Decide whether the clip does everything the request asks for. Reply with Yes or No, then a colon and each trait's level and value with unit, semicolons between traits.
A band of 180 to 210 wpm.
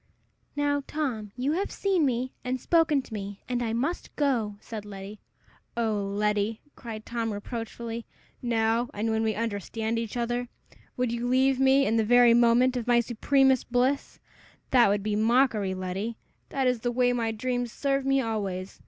No: average, 170 wpm